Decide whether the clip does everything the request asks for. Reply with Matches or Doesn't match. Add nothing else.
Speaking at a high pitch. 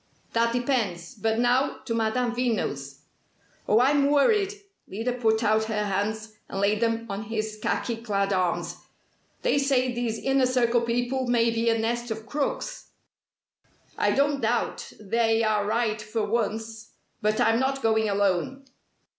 Matches